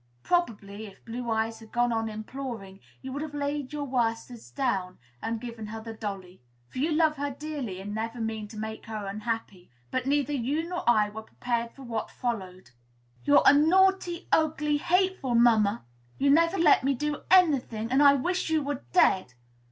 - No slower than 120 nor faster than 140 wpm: No, average, 185 wpm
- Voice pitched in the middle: No, high, 240 Hz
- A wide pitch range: No, average, 5.0 semitones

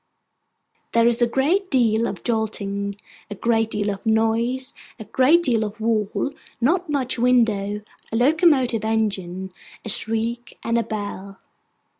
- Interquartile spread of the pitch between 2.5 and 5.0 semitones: Yes, average, 3.0 semitones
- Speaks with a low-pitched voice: No, high, 225 Hz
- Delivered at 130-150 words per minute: Yes, average, 140 wpm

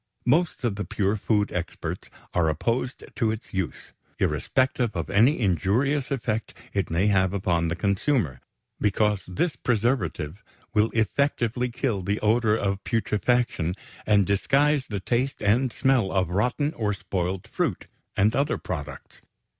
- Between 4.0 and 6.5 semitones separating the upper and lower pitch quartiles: Yes, average, 4.6 semitones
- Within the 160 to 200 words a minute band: No, average, 140 wpm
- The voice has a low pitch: Yes, low, 105 Hz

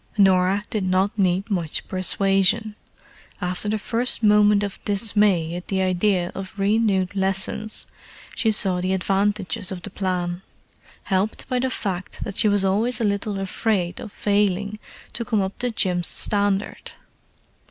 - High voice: Yes, high, 195 Hz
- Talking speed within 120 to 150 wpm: Yes, average, 145 wpm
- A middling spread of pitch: No, narrow, 2.1 semitones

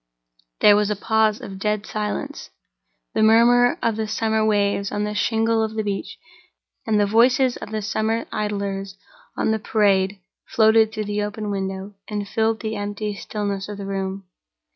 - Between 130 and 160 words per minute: No, average, 170 wpm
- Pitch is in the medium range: No, high, 210 Hz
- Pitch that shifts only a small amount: Yes, narrow, 1.5 semitones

